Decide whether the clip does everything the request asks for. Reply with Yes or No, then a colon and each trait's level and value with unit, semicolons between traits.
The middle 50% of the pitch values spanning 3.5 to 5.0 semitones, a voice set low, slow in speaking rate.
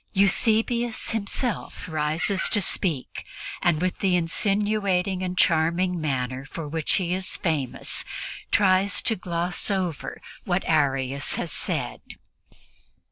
No: average, 3.8 semitones; medium, 180 Hz; slow, 115 wpm